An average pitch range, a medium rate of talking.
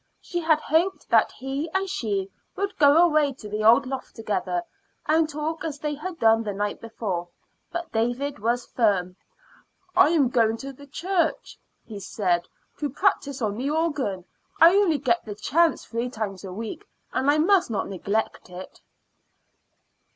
No: wide, 6.8 semitones; average, 165 wpm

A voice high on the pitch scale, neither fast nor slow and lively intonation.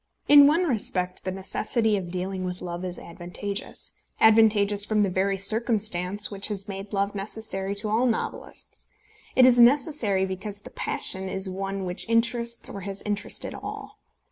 No: high, 200 Hz; average, 160 wpm; average, 2.7 semitones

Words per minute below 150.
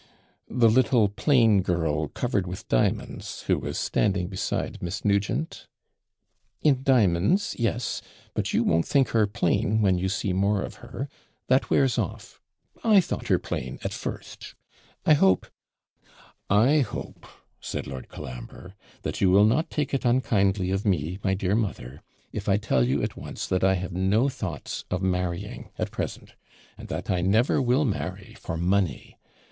No: average, 165 wpm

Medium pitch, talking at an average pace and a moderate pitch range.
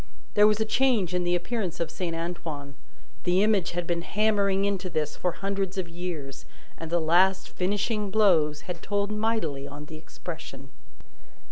Yes: medium, 180 Hz; average, 165 wpm; average, 3.5 semitones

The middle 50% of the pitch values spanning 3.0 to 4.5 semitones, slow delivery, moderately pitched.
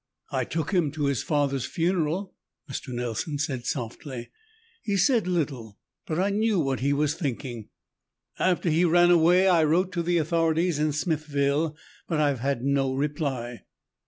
No: average, 4.1 semitones; average, 160 wpm; medium, 150 Hz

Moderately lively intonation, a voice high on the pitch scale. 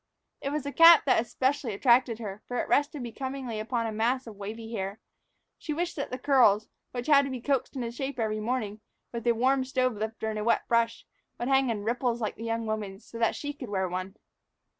Yes: average, 3.3 semitones; high, 235 Hz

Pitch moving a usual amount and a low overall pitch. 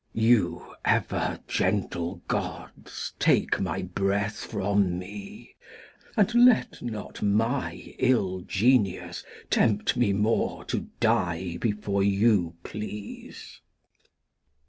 Yes: average, 3.2 semitones; low, 105 Hz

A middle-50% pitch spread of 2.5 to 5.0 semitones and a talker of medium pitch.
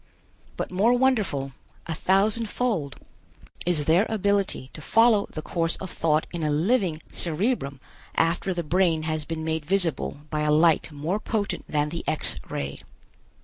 Yes: average, 4.7 semitones; medium, 165 Hz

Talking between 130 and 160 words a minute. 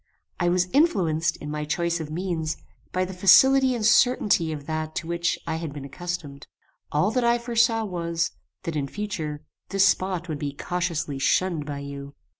No: average, 180 wpm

